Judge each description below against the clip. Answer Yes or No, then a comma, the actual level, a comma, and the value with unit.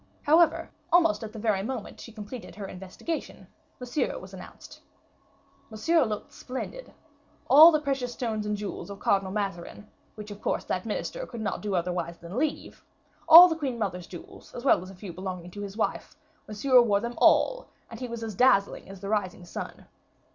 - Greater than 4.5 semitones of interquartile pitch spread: Yes, average, 4.9 semitones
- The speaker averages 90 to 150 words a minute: No, average, 185 wpm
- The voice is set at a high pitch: Yes, high, 215 Hz